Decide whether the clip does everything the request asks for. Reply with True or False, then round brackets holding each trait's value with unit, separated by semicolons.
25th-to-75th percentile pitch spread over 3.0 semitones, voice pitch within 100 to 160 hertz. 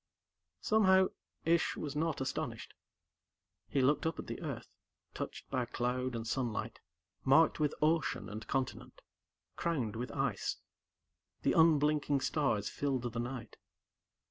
True (4.2 semitones; 135 Hz)